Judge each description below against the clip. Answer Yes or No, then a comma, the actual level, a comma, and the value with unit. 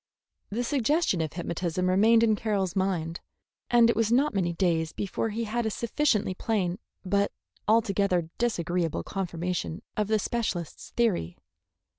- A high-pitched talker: Yes, high, 200 Hz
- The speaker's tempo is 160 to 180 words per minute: No, average, 140 wpm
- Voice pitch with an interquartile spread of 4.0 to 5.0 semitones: Yes, average, 4.6 semitones